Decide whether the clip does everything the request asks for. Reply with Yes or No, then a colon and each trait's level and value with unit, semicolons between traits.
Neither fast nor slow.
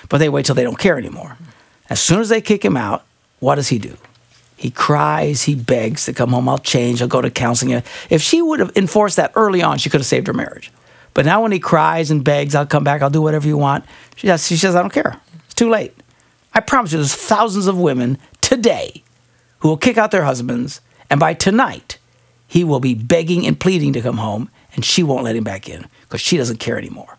No: fast, 235 wpm